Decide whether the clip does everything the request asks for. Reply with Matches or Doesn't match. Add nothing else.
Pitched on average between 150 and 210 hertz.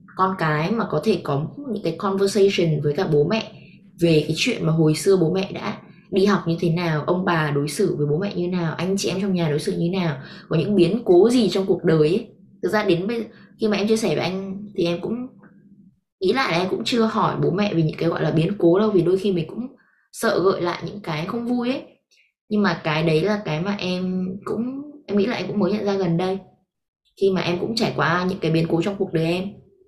Matches